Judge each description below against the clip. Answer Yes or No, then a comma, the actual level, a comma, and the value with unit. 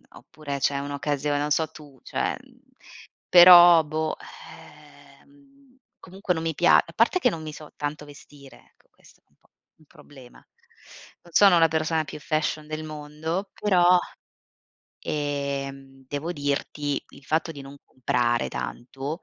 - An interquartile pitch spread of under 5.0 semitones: Yes, average, 2.7 semitones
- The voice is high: No, medium, 150 Hz